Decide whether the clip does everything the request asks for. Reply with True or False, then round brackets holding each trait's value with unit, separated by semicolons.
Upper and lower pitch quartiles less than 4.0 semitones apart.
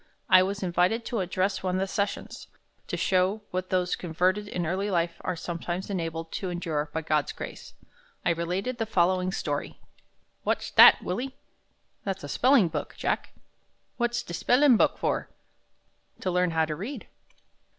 True (2.9 semitones)